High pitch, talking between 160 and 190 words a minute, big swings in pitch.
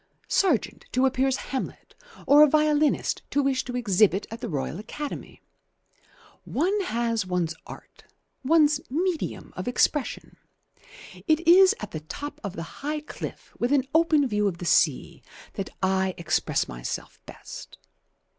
No: very high, 260 Hz; average, 145 wpm; wide, 7.1 semitones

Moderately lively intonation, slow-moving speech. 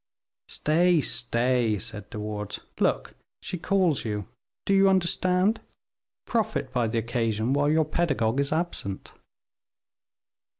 No: wide, 7.4 semitones; slow, 120 wpm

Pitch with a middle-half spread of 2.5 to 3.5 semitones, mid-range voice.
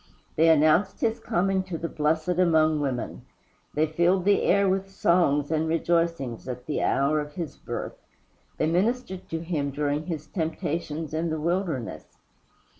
Yes: average, 3.0 semitones; medium, 160 Hz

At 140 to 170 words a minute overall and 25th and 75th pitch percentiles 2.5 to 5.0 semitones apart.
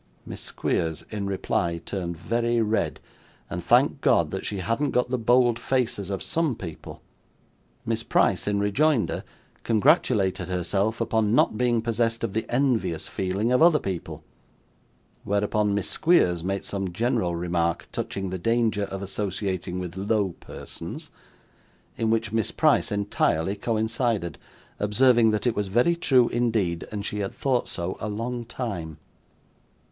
Yes: average, 145 wpm; average, 3.8 semitones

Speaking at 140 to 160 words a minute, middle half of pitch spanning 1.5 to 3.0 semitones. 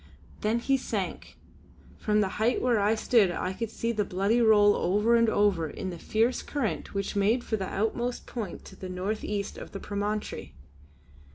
No: average, 185 wpm; narrow, 2.6 semitones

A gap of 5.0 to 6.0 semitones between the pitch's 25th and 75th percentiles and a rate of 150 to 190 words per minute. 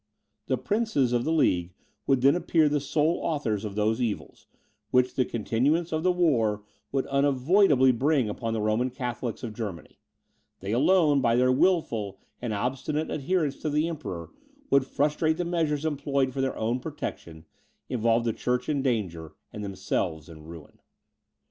Yes: wide, 5.5 semitones; average, 160 wpm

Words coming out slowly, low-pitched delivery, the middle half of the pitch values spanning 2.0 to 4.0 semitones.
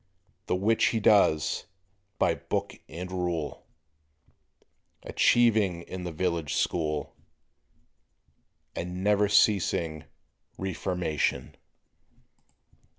Yes: slow, 80 wpm; very low, 90 Hz; average, 3.5 semitones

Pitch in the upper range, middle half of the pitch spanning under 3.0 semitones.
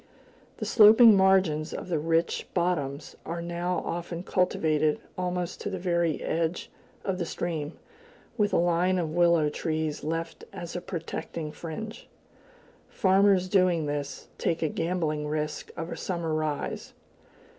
No: medium, 170 Hz; narrow, 2.6 semitones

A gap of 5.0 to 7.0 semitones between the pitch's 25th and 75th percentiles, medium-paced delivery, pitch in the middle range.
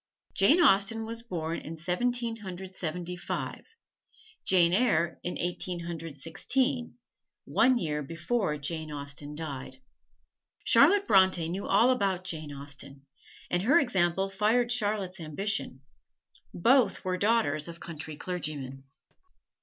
No: wide, 5.4 semitones; slow, 120 wpm; medium, 180 Hz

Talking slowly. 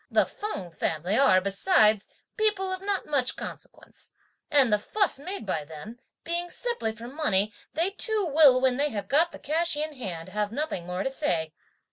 No: average, 180 wpm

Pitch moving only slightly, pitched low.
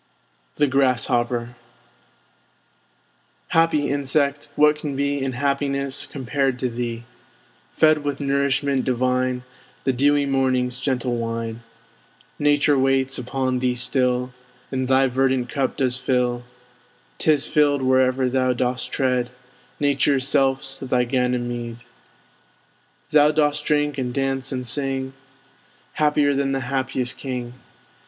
Yes: narrow, 1.9 semitones; low, 130 Hz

